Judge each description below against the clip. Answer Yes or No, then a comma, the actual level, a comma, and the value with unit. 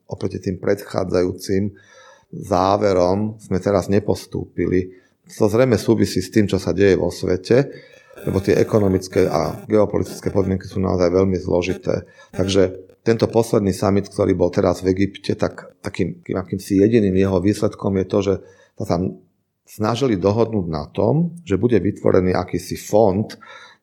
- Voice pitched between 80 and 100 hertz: Yes, very low, 95 Hz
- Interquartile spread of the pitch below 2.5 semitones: Yes, narrow, 2.0 semitones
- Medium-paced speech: Yes, average, 145 wpm